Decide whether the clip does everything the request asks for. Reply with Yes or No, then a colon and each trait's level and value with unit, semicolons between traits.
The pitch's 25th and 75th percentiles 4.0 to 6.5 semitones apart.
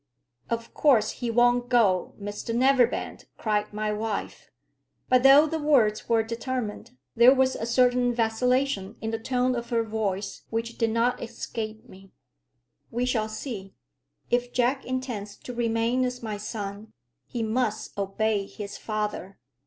No: average, 2.7 semitones